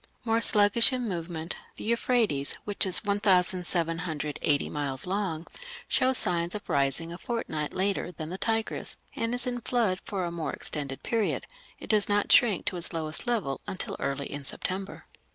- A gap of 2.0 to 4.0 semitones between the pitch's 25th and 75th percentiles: No, average, 5.3 semitones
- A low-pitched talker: No, medium, 185 Hz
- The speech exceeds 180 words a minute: No, average, 165 wpm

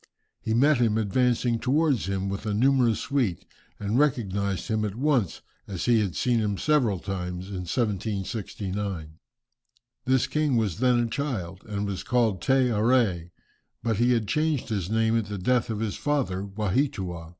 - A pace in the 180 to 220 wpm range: No, average, 165 wpm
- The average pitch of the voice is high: No, low, 110 Hz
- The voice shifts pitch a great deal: No, average, 4.2 semitones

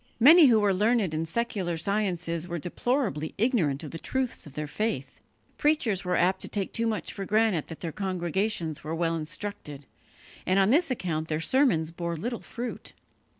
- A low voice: No, medium, 185 Hz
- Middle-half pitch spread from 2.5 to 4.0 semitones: No, wide, 5.6 semitones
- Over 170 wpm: Yes, average, 180 wpm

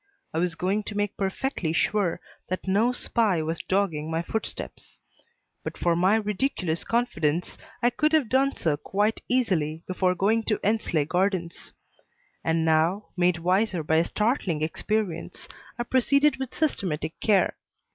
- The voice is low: No, high, 190 Hz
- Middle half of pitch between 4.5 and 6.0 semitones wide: Yes, average, 5.0 semitones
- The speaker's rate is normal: Yes, average, 145 wpm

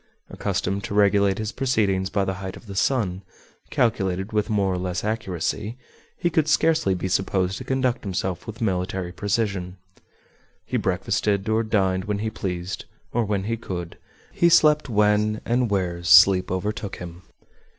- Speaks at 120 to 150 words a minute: No, average, 160 wpm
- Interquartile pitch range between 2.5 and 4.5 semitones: Yes, average, 2.8 semitones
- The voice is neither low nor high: No, low, 100 Hz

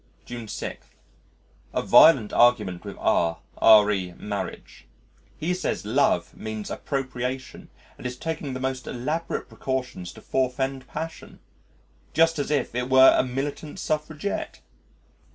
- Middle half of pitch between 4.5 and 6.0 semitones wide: No, average, 4.1 semitones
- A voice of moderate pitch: No, low, 130 Hz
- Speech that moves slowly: Yes, slow, 125 wpm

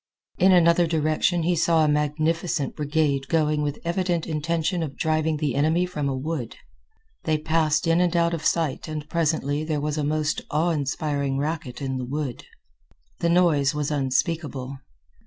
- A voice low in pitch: No, medium, 155 Hz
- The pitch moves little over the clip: Yes, narrow, 2.3 semitones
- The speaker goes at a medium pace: Yes, average, 165 wpm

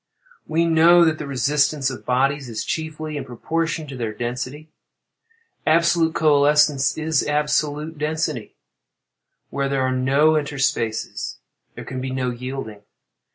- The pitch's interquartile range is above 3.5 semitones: No, average, 3.2 semitones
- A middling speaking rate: No, slow, 130 wpm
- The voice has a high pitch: No, medium, 145 Hz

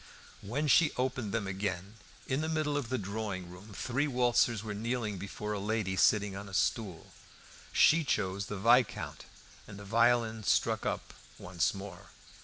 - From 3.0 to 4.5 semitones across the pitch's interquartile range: Yes, average, 3.7 semitones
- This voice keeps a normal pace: Yes, average, 165 wpm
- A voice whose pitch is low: Yes, low, 105 Hz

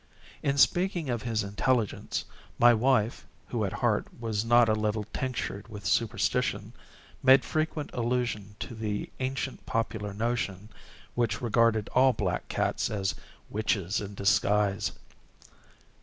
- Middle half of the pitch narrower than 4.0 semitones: Yes, average, 3.1 semitones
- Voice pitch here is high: No, low, 115 Hz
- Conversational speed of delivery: No, slow, 125 wpm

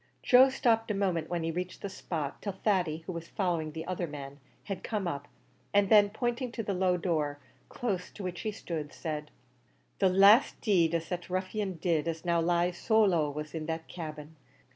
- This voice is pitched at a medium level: Yes, medium, 180 Hz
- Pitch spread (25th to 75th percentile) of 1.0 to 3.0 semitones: No, average, 3.7 semitones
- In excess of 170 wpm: Yes, average, 200 wpm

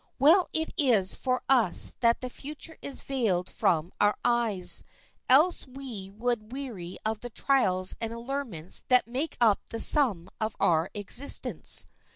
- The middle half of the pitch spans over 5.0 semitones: Yes, wide, 5.4 semitones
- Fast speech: No, average, 150 wpm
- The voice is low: No, high, 235 Hz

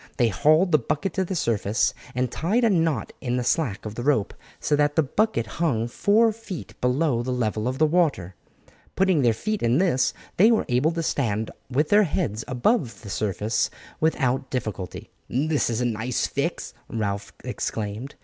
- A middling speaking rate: Yes, average, 180 wpm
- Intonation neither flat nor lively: No, wide, 6.4 semitones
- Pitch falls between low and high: No, low, 130 Hz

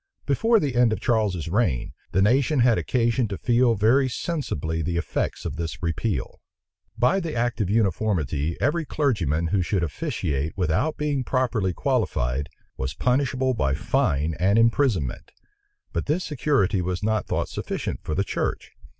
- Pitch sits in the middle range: No, low, 110 Hz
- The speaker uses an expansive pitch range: Yes, wide, 7.2 semitones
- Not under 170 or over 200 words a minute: No, average, 155 wpm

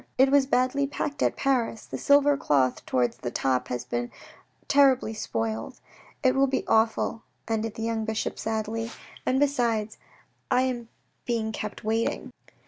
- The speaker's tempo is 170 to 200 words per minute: No, average, 155 wpm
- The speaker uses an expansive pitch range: No, average, 3.7 semitones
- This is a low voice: No, high, 225 Hz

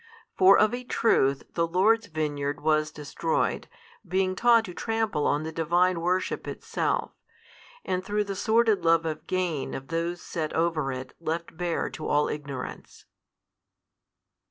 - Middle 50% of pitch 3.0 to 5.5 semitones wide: Yes, average, 3.8 semitones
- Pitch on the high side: No, medium, 170 Hz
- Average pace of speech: Yes, average, 145 wpm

